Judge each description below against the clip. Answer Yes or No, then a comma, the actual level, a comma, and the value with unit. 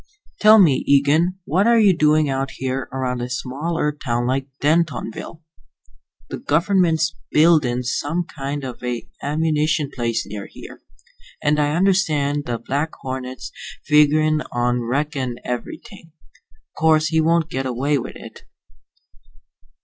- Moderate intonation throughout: Yes, average, 3.7 semitones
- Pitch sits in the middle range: Yes, medium, 145 Hz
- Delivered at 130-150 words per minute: Yes, slow, 135 wpm